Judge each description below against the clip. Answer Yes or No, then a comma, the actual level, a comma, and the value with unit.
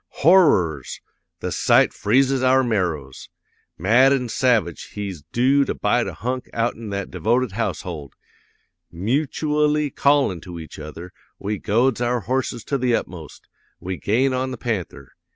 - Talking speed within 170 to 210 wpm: No, average, 140 wpm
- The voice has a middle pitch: No, low, 115 Hz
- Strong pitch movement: Yes, wide, 6.3 semitones